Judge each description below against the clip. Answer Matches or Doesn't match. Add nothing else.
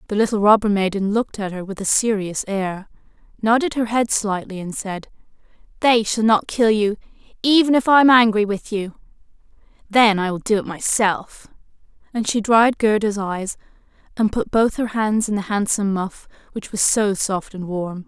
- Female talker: Matches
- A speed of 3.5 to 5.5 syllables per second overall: Matches